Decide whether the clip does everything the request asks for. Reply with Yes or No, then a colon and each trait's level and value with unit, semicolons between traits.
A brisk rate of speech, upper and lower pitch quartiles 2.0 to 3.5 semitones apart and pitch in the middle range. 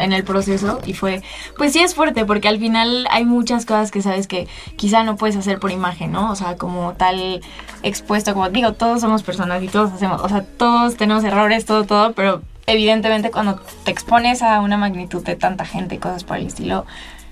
No: fast, 210 wpm; average, 2.9 semitones; high, 210 Hz